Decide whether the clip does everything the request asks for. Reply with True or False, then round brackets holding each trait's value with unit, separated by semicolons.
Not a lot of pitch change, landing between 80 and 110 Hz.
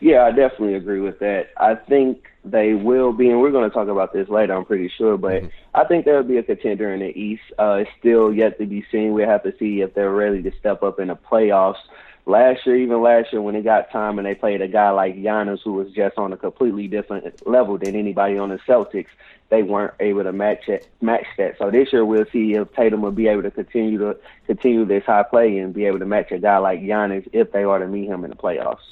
True (2.0 semitones; 105 Hz)